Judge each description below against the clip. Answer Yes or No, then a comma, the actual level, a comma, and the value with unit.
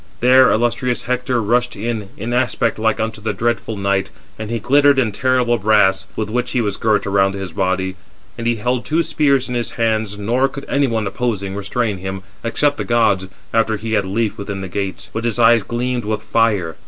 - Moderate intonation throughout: Yes, average, 3.3 semitones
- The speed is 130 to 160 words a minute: No, fast, 205 wpm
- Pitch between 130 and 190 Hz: No, low, 110 Hz